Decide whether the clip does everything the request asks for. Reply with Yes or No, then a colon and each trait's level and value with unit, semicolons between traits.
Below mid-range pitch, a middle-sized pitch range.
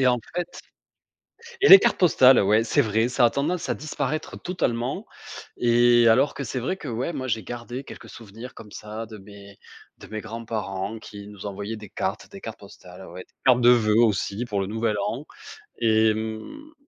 Yes: low, 115 Hz; average, 3.1 semitones